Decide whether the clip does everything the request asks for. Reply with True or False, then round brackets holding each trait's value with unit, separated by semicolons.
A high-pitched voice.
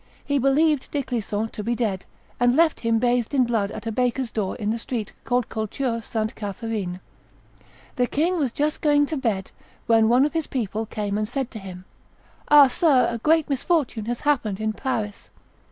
True (235 Hz)